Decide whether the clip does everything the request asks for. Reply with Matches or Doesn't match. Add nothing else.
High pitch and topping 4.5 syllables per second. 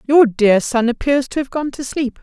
Matches